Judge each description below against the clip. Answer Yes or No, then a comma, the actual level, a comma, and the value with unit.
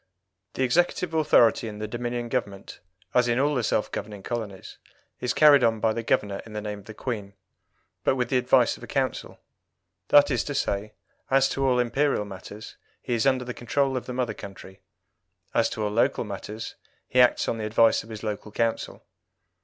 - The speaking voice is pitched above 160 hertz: No, low, 115 Hz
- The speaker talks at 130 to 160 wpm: No, average, 200 wpm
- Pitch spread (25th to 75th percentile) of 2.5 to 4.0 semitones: Yes, average, 3.2 semitones